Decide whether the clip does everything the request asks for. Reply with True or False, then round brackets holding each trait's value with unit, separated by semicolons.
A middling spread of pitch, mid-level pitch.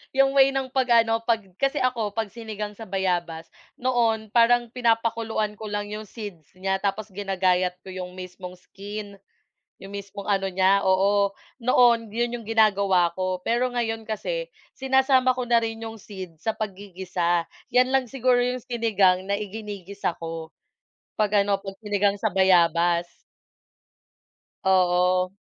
False (3.6 semitones; 205 Hz)